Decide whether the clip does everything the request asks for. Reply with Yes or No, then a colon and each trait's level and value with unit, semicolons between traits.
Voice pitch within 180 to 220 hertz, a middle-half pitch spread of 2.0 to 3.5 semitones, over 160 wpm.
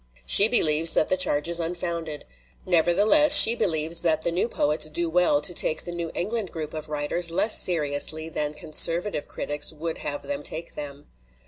No: medium, 165 Hz; narrow, 2.5 semitones; average, 180 wpm